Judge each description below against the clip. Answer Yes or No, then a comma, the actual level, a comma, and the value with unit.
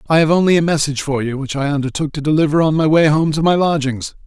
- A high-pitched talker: No, medium, 150 Hz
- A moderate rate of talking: No, fast, 265 wpm